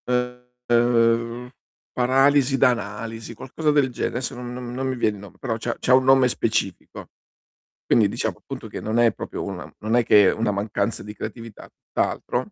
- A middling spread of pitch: No, narrow, 2.3 semitones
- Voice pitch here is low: Yes, low, 120 Hz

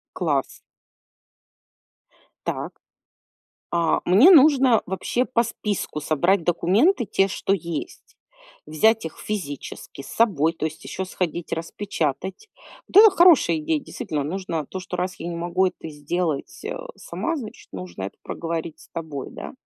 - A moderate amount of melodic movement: No, wide, 6.4 semitones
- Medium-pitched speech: Yes, medium, 180 Hz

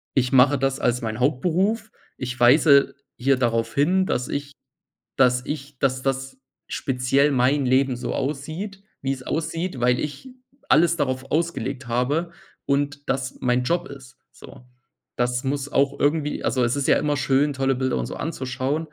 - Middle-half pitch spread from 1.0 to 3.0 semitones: Yes, narrow, 2.5 semitones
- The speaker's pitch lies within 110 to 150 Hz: Yes, low, 135 Hz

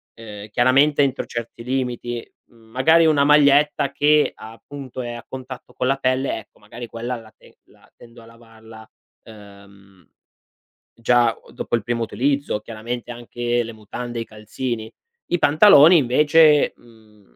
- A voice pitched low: Yes, low, 120 Hz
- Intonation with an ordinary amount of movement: Yes, average, 3.5 semitones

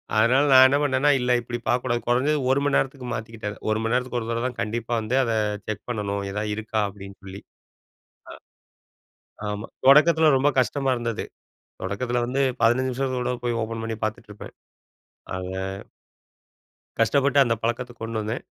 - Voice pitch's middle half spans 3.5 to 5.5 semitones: No, average, 3.1 semitones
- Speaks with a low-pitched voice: Yes, low, 120 Hz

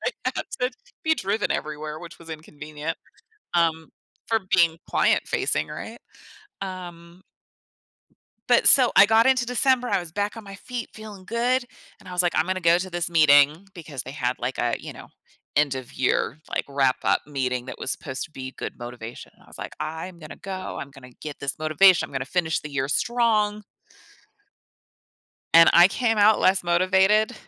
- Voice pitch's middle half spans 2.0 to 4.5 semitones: No, wide, 5.6 semitones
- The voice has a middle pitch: Yes, medium, 170 Hz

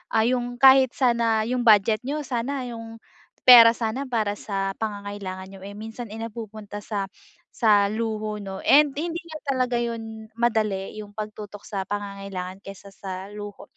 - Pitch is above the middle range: Yes, high, 220 Hz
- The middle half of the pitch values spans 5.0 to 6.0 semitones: No, average, 2.8 semitones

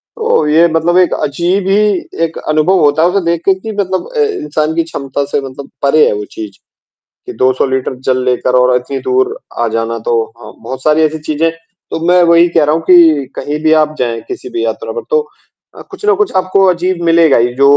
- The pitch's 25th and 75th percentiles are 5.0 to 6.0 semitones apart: Yes, average, 5.3 semitones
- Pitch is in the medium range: Yes, medium, 155 Hz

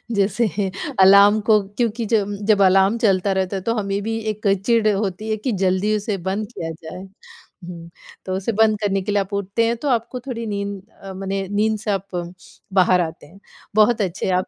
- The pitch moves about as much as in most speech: No, narrow, 2.1 semitones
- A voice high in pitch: Yes, high, 200 Hz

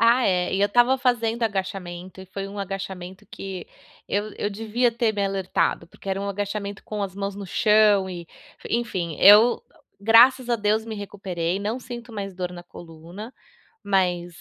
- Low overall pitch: No, high, 200 Hz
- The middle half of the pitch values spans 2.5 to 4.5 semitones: Yes, average, 2.9 semitones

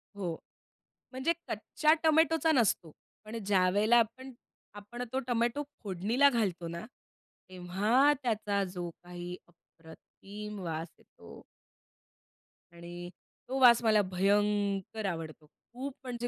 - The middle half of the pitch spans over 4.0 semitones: Yes, wide, 5.4 semitones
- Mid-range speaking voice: No, high, 210 Hz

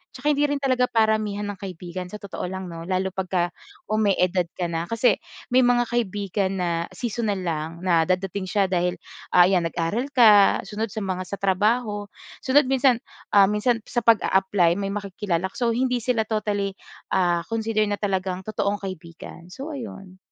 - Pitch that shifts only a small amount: No, average, 3.6 semitones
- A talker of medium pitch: No, high, 200 Hz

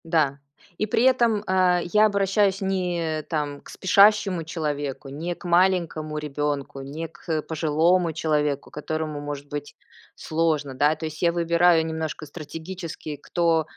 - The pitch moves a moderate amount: Yes, average, 3.1 semitones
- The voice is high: No, medium, 160 Hz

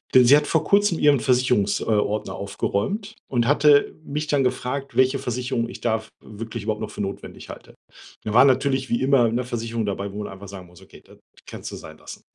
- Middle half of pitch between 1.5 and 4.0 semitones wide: No, average, 4.4 semitones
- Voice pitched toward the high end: No, low, 125 Hz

